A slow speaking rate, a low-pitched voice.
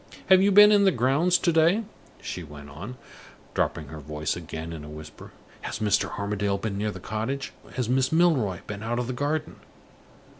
No: average, 190 wpm; low, 110 Hz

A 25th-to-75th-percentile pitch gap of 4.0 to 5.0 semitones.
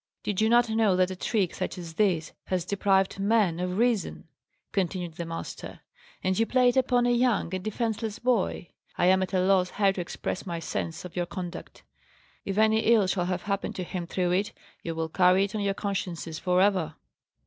No: average, 3.2 semitones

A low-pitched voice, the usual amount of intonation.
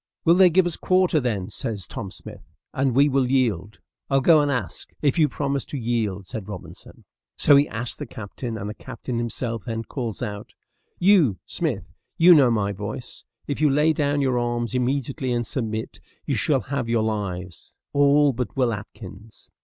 Yes: low, 125 Hz; average, 4.4 semitones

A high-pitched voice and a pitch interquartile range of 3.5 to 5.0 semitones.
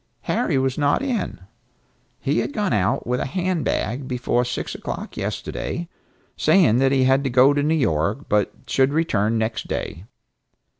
No: low, 130 Hz; average, 4.2 semitones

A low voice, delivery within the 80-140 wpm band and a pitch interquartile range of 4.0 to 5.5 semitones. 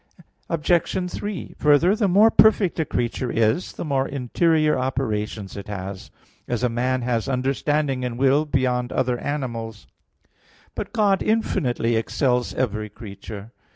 Yes: low, 130 Hz; slow, 135 wpm; average, 4.8 semitones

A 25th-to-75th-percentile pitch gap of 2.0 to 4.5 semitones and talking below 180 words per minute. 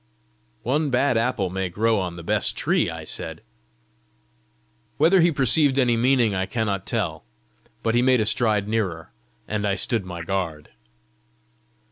No: average, 4.9 semitones; average, 155 wpm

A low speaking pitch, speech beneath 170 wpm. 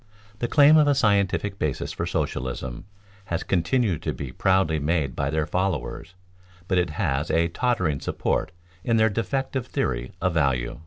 Yes: very low, 85 Hz; average, 160 wpm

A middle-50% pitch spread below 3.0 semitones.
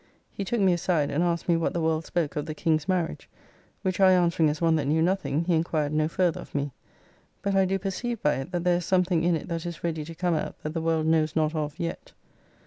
Yes: narrow, 2.4 semitones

